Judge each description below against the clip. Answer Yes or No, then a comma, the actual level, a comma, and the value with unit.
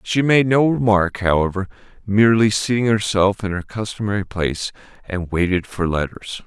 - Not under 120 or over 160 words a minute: Yes, average, 150 wpm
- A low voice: Yes, low, 100 Hz